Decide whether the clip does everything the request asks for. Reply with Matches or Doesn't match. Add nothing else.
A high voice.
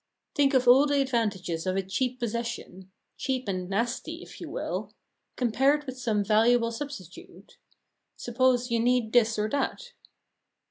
Matches